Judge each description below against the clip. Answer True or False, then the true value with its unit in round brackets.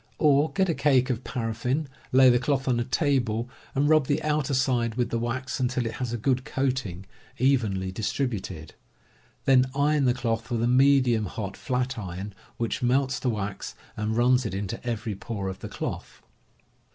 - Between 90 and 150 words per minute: False (175 wpm)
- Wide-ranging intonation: False (3.0 semitones)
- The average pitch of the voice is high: False (125 Hz)